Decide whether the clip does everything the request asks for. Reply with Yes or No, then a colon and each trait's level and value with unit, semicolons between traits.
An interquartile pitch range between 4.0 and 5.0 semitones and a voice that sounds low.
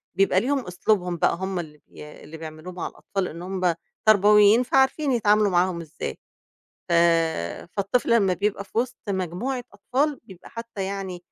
No: average, 4.3 semitones; high, 195 Hz